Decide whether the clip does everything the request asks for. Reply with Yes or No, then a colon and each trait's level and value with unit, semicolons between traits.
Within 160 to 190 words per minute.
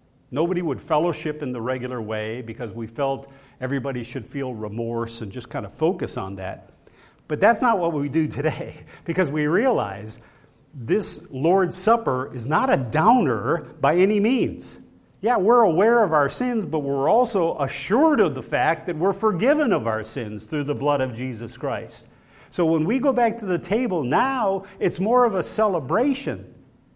Yes: average, 180 wpm